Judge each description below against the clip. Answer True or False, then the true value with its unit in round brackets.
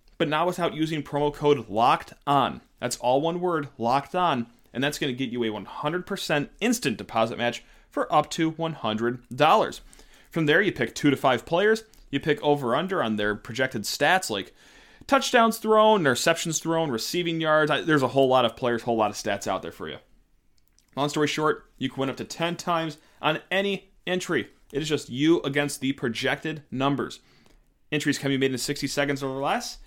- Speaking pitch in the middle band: True (145 Hz)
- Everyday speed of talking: True (195 wpm)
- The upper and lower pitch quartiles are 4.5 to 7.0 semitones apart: True (4.9 semitones)